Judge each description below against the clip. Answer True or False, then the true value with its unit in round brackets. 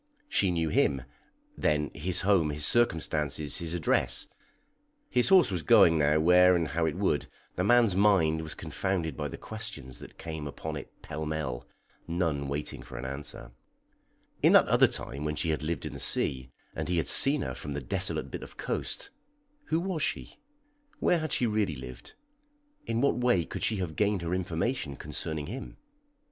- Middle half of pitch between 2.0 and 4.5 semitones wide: False (5.1 semitones)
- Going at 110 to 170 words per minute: False (180 wpm)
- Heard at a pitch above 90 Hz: False (80 Hz)